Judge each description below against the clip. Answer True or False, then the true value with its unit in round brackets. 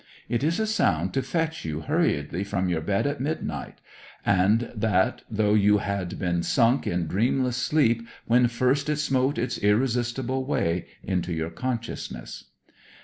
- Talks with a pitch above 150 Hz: False (115 Hz)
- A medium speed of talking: True (150 wpm)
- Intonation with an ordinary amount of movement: False (6.0 semitones)